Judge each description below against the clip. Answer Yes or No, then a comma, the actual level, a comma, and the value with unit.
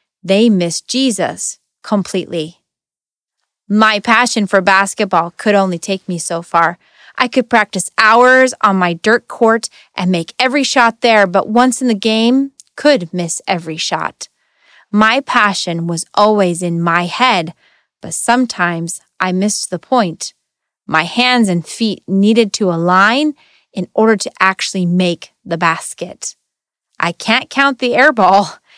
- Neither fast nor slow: Yes, average, 145 wpm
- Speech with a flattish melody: No, average, 5.2 semitones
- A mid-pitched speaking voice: No, high, 200 Hz